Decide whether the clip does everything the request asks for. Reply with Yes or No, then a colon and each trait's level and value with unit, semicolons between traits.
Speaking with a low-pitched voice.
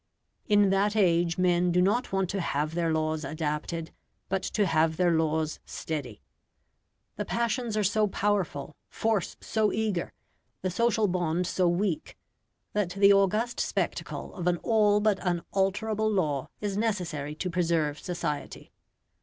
No: medium, 180 Hz